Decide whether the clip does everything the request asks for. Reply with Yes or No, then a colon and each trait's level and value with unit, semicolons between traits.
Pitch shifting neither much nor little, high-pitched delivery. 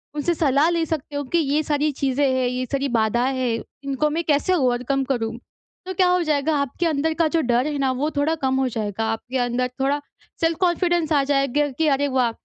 Yes: average, 3.4 semitones; very high, 280 Hz